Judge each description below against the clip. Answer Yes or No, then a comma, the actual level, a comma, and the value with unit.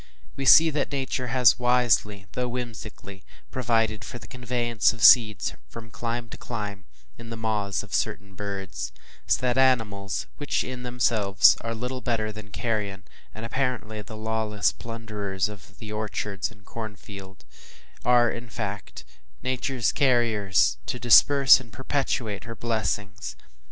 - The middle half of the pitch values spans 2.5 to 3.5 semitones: Yes, average, 3.1 semitones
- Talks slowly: No, average, 145 wpm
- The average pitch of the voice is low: Yes, low, 115 Hz